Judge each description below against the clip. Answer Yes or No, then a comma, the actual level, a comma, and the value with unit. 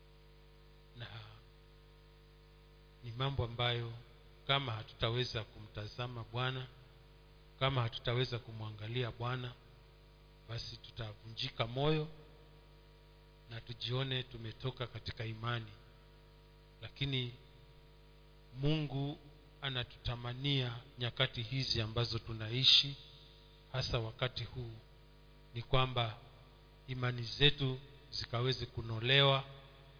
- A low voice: Yes, low, 130 Hz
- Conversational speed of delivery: No, slow, 70 wpm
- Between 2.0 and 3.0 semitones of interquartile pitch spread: No, average, 4.3 semitones